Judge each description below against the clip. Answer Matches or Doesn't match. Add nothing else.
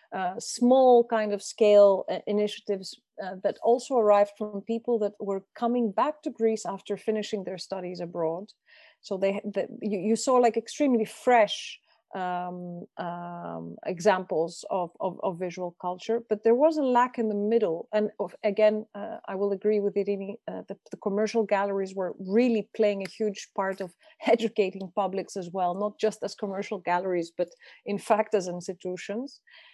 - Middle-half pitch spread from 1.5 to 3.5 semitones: Matches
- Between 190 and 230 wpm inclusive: Doesn't match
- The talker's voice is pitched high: Matches